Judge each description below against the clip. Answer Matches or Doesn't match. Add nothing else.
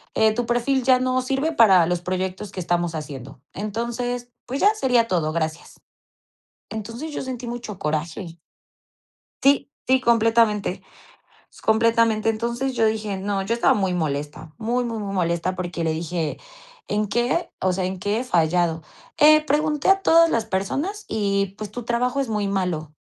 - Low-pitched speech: Doesn't match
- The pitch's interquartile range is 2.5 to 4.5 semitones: Doesn't match